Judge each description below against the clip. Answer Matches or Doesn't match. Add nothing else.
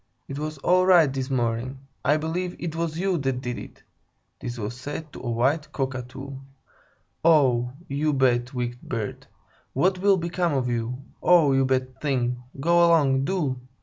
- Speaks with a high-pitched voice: Doesn't match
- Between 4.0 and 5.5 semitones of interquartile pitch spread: Matches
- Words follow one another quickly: Doesn't match